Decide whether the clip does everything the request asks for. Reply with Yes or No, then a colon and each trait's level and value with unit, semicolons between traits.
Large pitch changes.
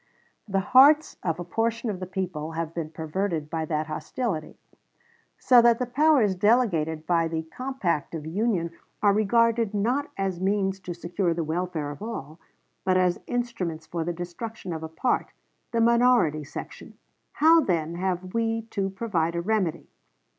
Yes: wide, 5.7 semitones